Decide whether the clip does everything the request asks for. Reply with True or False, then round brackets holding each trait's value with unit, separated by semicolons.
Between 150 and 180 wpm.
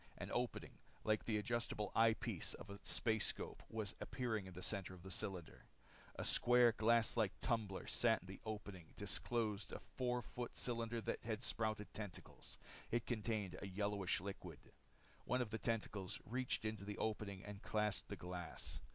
True (170 wpm)